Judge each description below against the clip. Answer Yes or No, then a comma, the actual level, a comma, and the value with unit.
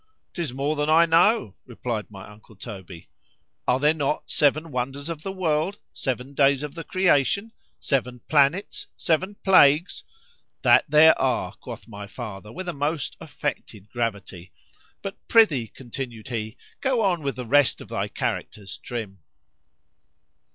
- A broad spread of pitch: Yes, wide, 6.2 semitones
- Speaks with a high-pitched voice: No, medium, 140 Hz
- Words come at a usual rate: No, slow, 130 wpm